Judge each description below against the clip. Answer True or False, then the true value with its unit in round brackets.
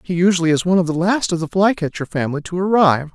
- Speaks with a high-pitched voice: False (175 Hz)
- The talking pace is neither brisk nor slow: False (250 wpm)